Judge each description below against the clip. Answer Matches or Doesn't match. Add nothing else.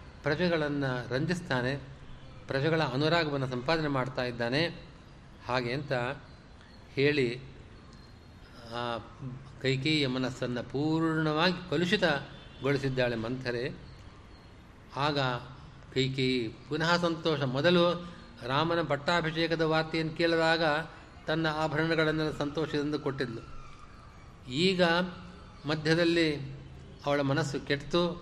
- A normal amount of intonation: Matches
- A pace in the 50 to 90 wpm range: Matches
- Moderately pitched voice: Matches